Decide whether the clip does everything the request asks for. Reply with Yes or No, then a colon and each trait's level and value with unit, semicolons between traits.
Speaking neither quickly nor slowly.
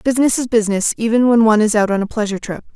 No: fast, 260 wpm